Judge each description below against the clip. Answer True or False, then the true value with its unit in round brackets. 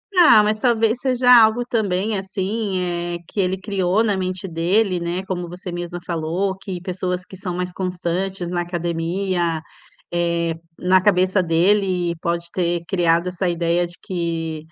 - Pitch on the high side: False (180 Hz)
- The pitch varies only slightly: True (2.1 semitones)